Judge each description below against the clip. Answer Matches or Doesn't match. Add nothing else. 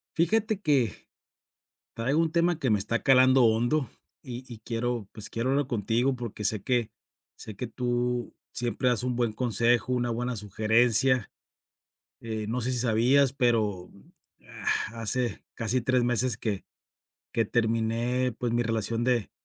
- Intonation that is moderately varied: Doesn't match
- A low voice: Matches